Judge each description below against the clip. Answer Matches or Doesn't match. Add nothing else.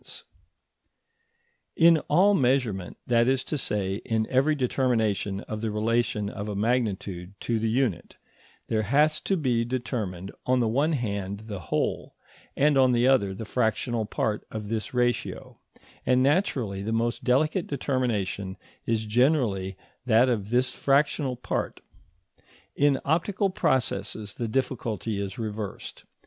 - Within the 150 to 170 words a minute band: Doesn't match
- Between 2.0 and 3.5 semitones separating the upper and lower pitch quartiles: Doesn't match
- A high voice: Doesn't match